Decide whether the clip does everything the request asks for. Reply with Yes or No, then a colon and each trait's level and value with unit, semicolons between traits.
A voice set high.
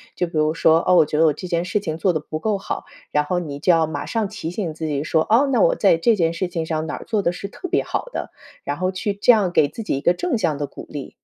No: medium, 170 Hz